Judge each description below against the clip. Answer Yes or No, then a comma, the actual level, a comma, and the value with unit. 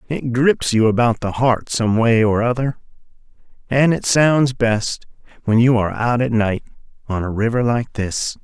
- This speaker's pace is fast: No, average, 180 wpm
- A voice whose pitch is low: Yes, low, 120 Hz